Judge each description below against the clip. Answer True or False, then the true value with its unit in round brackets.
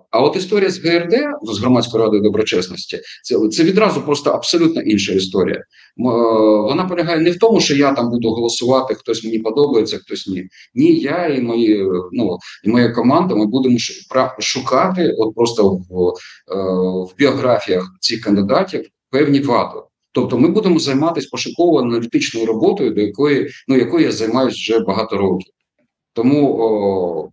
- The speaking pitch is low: True (120 Hz)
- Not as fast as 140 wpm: False (150 wpm)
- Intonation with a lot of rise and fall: True (6.6 semitones)